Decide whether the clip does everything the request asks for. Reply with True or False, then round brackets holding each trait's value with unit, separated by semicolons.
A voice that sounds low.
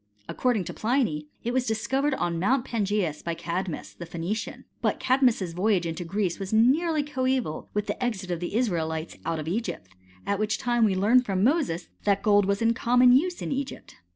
False (210 Hz)